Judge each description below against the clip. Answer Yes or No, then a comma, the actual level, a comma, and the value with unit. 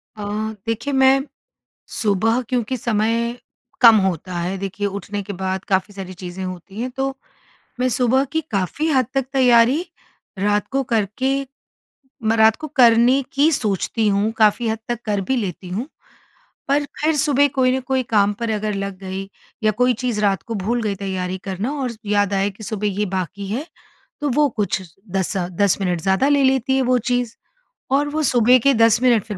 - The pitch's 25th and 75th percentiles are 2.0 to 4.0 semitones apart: No, average, 4.5 semitones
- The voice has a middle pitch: No, high, 225 Hz